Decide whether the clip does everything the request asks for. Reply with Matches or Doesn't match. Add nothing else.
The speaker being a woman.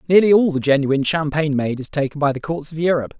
Doesn't match